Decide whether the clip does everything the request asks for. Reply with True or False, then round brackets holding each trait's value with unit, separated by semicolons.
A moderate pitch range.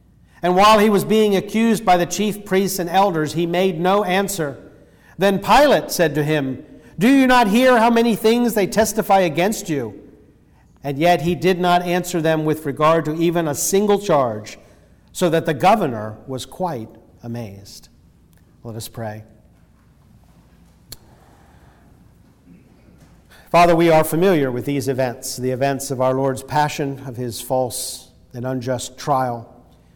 False (6.7 semitones)